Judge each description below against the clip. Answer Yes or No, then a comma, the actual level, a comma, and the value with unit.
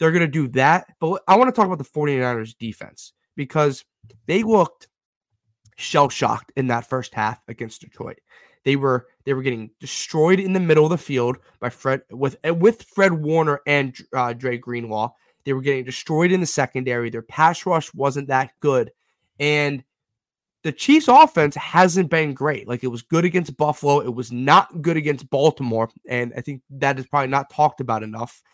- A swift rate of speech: No, average, 185 wpm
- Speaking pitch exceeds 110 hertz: Yes, medium, 140 Hz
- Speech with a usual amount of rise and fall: Yes, average, 4.3 semitones